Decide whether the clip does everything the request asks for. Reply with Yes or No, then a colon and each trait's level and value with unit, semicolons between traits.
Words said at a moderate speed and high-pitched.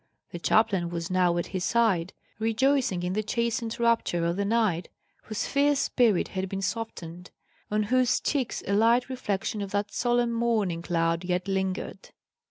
Yes: average, 165 wpm; high, 205 Hz